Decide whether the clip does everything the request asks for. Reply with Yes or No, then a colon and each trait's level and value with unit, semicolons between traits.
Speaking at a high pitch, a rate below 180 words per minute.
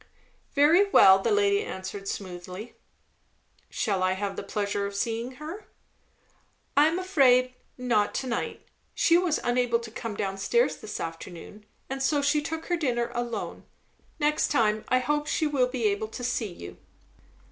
Yes: high, 240 Hz; average, 160 wpm